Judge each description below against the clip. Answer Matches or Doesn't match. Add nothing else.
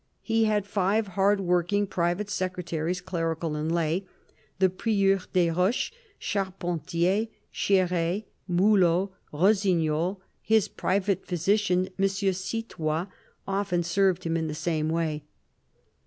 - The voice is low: Doesn't match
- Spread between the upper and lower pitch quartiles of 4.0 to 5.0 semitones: Doesn't match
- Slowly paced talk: Matches